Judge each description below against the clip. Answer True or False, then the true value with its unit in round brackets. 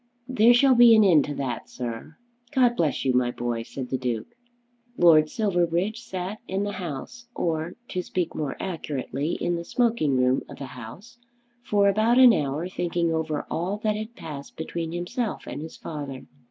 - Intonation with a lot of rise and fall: True (7.0 semitones)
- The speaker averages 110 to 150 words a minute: False (180 wpm)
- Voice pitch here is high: False (170 Hz)